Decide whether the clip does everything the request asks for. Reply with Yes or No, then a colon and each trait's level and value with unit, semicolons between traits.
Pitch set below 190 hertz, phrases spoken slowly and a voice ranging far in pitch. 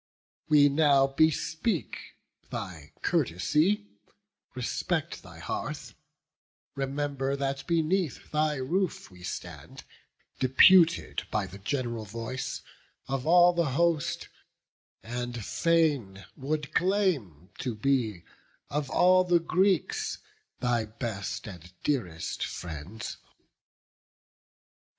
Yes: low, 135 Hz; slow, 95 wpm; wide, 6.6 semitones